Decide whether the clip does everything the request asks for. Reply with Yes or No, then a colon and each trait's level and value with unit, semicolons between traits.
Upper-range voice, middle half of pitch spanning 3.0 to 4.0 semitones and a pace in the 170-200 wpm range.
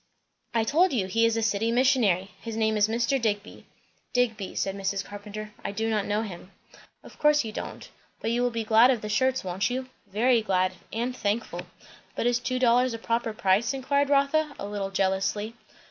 Yes: high, 225 Hz; average, 3.3 semitones; average, 195 wpm